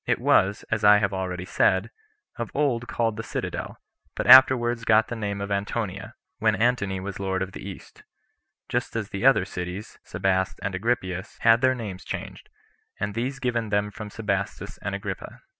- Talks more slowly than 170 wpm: No, average, 175 wpm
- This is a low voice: Yes, low, 105 Hz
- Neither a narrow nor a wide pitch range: Yes, average, 3.3 semitones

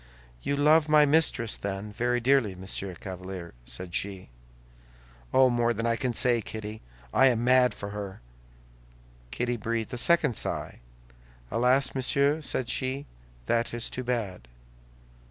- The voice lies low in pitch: Yes, low, 120 Hz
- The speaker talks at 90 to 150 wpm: Yes, average, 140 wpm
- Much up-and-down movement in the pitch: No, average, 4.4 semitones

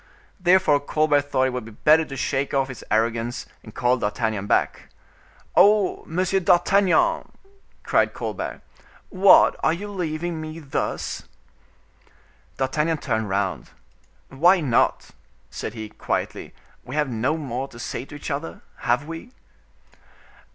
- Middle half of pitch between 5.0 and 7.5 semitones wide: Yes, wide, 5.5 semitones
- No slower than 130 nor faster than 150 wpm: Yes, slow, 135 wpm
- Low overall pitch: No, medium, 145 Hz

